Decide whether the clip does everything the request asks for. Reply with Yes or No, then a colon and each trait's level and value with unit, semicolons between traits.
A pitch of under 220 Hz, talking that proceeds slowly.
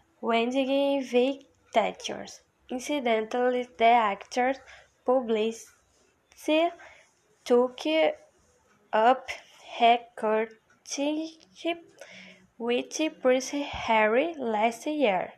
No: very high, 255 Hz; slow, 60 wpm